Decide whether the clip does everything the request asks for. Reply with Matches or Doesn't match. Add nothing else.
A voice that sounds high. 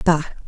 Doesn't match